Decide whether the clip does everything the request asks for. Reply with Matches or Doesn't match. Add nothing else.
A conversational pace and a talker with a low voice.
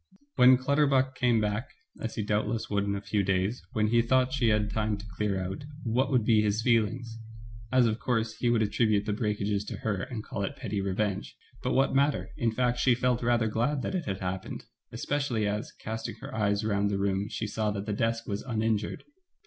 Doesn't match